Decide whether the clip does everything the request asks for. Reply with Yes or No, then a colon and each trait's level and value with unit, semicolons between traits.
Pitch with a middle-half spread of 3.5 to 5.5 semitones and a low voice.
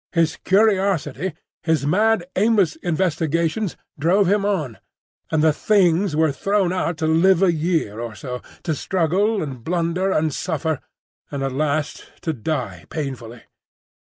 No: average, 4.2 semitones; medium, 165 Hz